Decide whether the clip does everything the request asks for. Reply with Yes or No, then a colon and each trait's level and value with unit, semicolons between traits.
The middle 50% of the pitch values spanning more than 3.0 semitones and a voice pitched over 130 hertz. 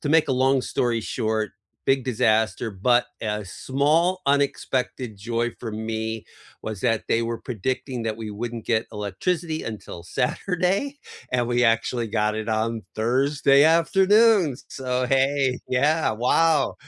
No: average, 4.2 semitones; low, 125 Hz